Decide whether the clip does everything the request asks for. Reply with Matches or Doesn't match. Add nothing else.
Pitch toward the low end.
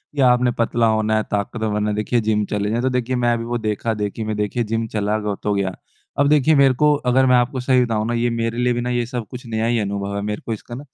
Matches